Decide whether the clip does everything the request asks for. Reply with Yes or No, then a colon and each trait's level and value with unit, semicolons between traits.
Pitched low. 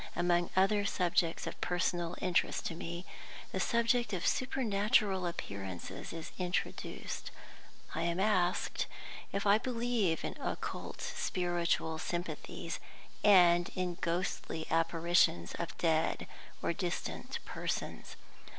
No: medium, 175 Hz